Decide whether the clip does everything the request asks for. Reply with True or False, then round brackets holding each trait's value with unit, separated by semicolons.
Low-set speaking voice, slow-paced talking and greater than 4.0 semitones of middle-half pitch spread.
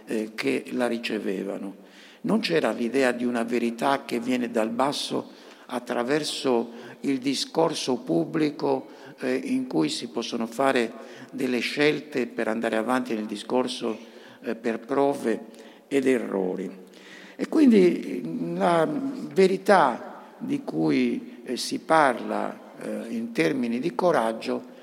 True (125 Hz; 110 wpm; 4.5 semitones)